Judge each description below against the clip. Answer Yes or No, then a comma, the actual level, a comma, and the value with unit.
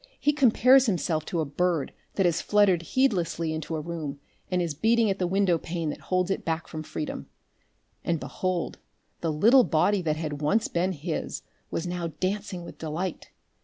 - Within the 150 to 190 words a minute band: Yes, average, 180 wpm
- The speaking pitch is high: No, medium, 175 Hz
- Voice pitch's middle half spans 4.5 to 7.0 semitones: No, average, 3.6 semitones